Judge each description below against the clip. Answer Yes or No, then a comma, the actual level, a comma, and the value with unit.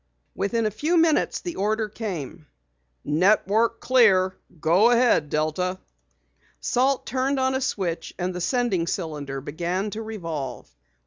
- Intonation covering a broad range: Yes, wide, 6.1 semitones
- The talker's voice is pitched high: Yes, high, 200 Hz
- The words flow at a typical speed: No, slow, 130 wpm